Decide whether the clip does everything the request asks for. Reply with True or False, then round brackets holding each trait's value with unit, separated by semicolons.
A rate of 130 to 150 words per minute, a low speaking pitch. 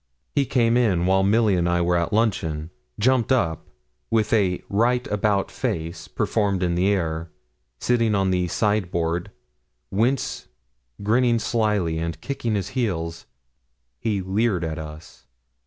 True (140 wpm; 100 Hz)